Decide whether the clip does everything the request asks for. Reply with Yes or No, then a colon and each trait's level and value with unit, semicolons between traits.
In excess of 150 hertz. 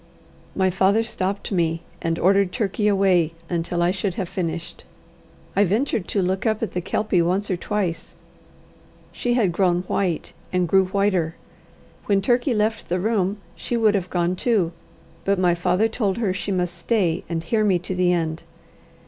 Yes: high, 190 Hz